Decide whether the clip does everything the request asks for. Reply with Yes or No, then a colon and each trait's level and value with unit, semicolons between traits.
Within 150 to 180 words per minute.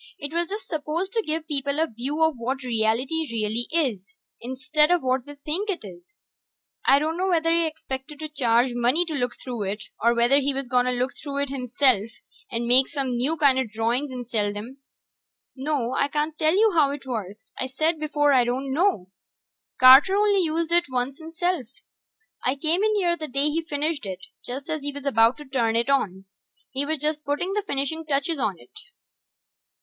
No: average, 195 wpm